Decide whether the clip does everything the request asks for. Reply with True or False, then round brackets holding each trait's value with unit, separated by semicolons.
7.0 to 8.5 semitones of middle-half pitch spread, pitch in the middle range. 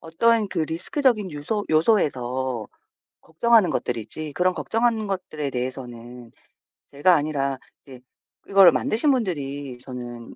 True (7.4 semitones; 155 Hz)